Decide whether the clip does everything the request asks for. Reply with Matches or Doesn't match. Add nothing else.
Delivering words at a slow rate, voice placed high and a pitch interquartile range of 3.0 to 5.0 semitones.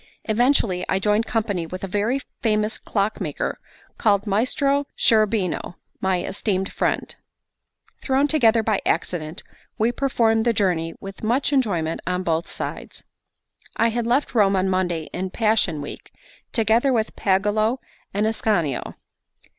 Matches